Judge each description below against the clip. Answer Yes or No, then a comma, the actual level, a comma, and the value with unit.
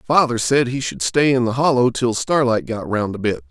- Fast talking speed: Yes, fast, 240 wpm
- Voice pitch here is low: Yes, low, 120 Hz